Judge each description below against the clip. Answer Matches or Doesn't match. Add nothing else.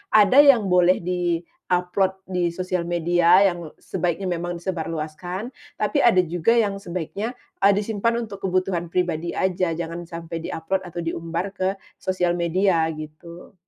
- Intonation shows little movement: Matches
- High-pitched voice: Doesn't match